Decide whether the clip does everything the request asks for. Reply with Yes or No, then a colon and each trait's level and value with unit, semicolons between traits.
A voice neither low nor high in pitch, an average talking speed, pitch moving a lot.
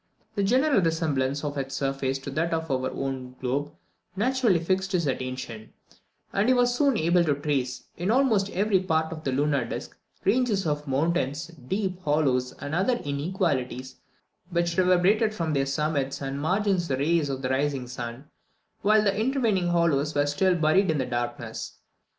Yes: medium, 160 Hz; average, 165 wpm; wide, 5.8 semitones